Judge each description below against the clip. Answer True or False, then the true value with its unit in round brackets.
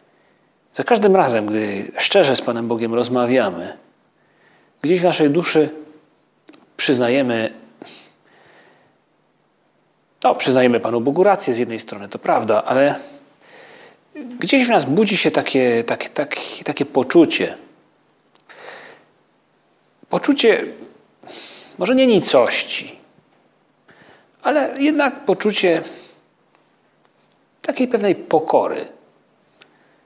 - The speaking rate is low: True (90 wpm)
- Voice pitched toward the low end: False (175 Hz)